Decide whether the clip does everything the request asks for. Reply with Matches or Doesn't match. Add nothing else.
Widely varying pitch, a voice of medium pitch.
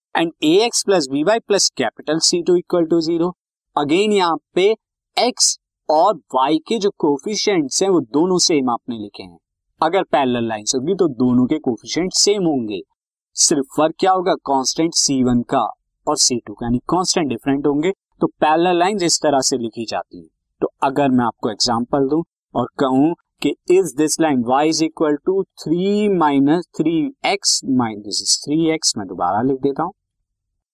Matches